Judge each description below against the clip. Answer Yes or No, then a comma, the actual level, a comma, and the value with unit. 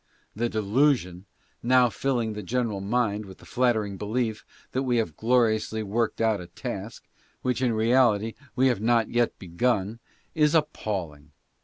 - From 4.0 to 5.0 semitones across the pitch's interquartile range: No, average, 3.3 semitones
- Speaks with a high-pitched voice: No, low, 110 Hz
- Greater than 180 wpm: No, average, 150 wpm